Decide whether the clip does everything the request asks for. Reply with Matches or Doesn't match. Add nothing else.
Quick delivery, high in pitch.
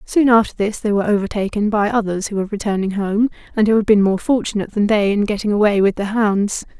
Matches